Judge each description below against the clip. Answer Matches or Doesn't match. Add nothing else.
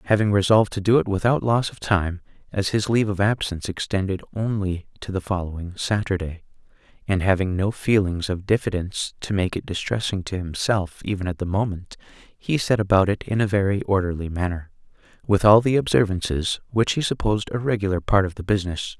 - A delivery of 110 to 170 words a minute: Doesn't match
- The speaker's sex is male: Matches